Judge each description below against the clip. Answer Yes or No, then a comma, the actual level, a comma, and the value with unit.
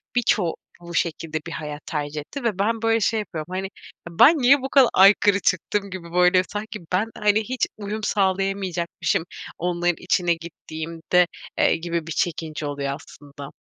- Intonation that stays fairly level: No, average, 4.1 semitones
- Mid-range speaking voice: Yes, medium, 180 Hz